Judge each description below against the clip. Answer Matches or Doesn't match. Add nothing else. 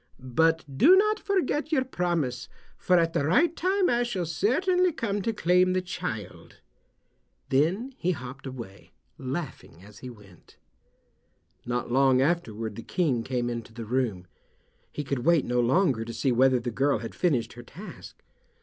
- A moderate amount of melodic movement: Doesn't match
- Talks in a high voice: Doesn't match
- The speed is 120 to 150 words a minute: Doesn't match